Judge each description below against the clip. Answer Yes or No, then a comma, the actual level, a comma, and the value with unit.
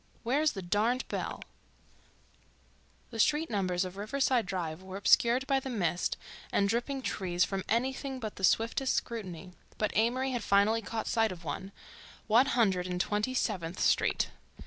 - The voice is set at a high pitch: Yes, high, 215 Hz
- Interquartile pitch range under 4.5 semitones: No, average, 4.9 semitones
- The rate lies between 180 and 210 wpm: No, average, 150 wpm